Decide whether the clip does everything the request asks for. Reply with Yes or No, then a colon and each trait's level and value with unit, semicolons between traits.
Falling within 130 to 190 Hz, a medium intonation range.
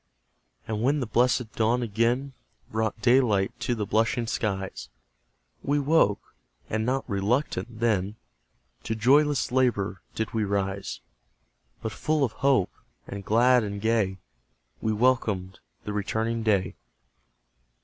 No: low, 110 Hz; average, 3.5 semitones